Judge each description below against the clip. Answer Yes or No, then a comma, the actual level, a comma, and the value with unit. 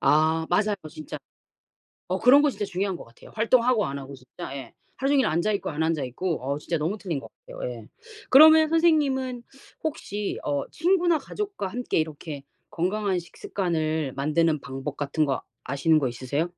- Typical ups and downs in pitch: No, wide, 9.0 semitones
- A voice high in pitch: No, medium, 175 Hz